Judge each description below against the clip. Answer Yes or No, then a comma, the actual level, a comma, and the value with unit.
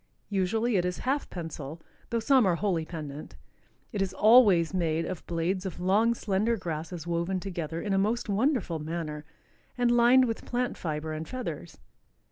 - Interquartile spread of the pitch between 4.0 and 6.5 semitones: Yes, wide, 5.4 semitones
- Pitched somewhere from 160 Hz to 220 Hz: Yes, medium, 185 Hz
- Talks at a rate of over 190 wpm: No, average, 165 wpm